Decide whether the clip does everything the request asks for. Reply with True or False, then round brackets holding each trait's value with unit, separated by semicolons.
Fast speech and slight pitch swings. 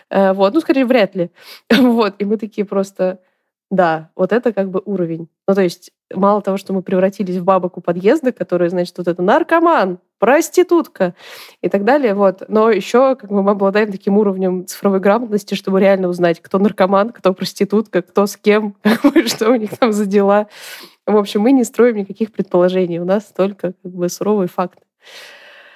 False (180 wpm; 3.1 semitones)